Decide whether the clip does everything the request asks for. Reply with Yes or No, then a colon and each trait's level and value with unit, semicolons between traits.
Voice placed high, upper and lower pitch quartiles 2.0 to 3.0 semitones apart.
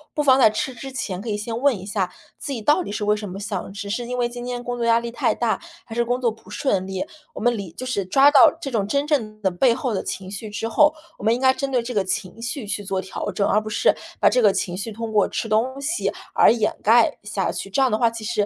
No: high, 230 Hz; average, 3.4 semitones